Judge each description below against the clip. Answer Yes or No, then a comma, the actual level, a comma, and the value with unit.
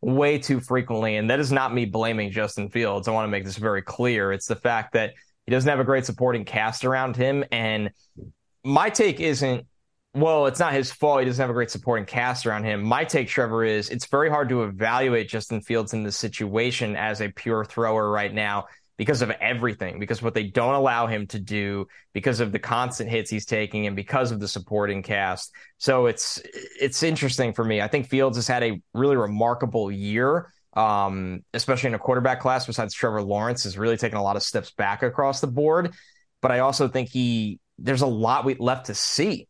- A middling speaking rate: No, fast, 215 wpm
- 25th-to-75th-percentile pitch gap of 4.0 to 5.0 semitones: No, average, 3.5 semitones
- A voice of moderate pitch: No, low, 115 Hz